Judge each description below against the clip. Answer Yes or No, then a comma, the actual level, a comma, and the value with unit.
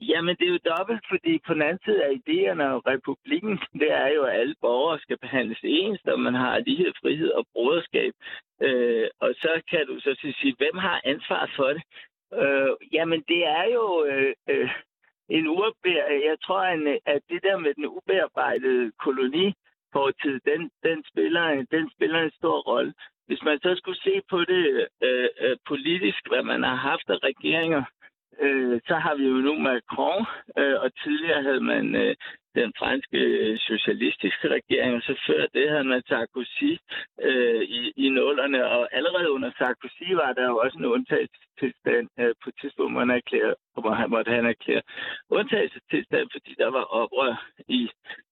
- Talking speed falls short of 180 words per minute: Yes, average, 170 wpm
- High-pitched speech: Yes, very high, 255 Hz